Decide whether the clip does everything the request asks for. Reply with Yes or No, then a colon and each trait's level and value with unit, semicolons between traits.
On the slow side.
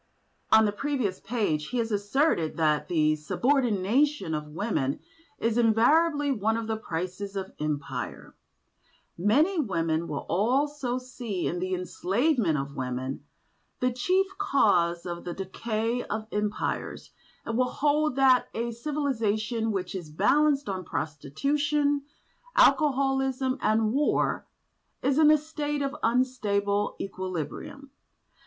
Yes: slow, 125 wpm